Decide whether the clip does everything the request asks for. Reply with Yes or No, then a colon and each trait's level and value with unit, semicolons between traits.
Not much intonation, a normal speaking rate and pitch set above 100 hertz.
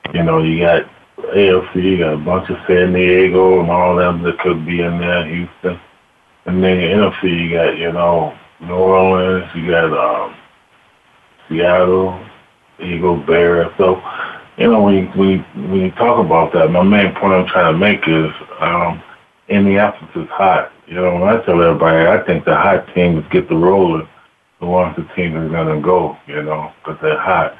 No: narrow, 1.8 semitones; average, 195 wpm; very low, 90 Hz